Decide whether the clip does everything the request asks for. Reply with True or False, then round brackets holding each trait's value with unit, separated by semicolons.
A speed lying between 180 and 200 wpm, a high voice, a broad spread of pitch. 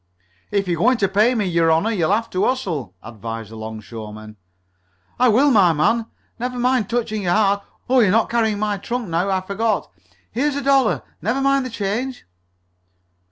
True (185 wpm; 210 Hz; 6.2 semitones)